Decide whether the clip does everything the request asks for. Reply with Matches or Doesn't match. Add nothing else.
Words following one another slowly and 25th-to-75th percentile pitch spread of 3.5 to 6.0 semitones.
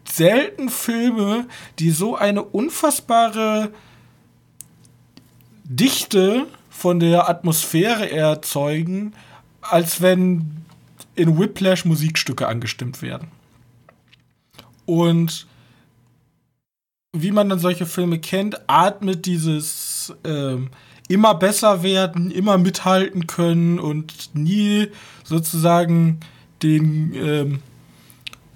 Matches